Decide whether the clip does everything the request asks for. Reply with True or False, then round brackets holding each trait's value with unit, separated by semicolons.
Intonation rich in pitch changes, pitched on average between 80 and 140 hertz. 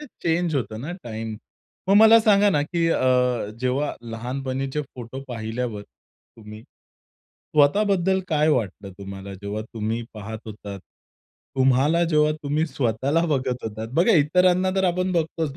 True (6.9 semitones; 135 Hz)